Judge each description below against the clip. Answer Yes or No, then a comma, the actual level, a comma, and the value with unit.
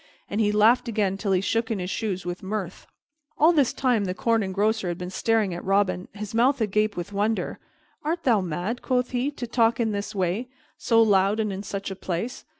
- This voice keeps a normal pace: No, fast, 215 wpm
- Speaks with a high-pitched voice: Yes, high, 210 Hz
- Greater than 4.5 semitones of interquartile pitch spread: No, average, 3.2 semitones